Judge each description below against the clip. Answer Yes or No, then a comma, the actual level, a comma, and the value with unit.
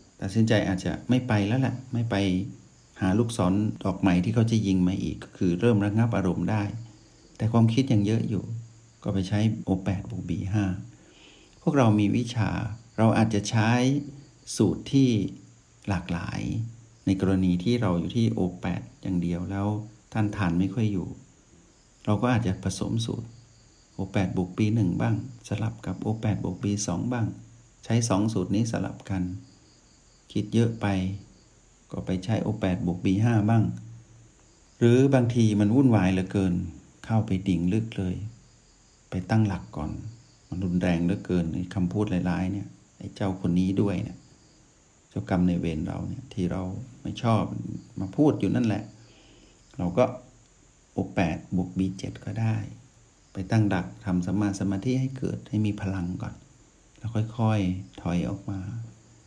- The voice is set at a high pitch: No, low, 105 Hz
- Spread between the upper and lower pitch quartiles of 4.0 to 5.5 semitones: No, average, 3.4 semitones